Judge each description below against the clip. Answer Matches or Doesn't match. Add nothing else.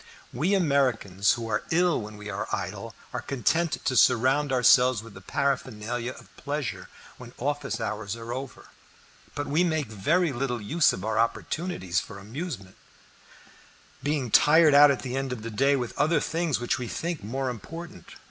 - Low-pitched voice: Matches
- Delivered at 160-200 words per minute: Matches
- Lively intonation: Doesn't match